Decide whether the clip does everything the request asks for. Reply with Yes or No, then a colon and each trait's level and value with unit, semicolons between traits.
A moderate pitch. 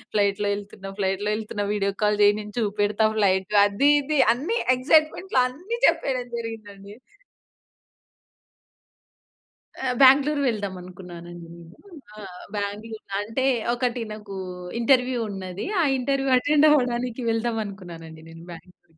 No: high, 210 Hz